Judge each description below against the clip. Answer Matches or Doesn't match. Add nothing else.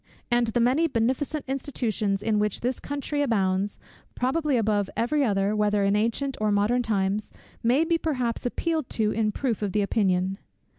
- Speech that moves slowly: Doesn't match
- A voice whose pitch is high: Matches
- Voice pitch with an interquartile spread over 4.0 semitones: Matches